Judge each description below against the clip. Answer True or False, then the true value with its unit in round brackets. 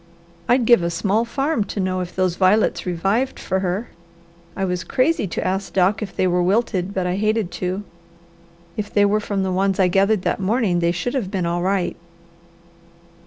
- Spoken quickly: False (195 wpm)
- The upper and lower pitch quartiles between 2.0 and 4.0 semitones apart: True (2.8 semitones)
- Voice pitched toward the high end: True (195 Hz)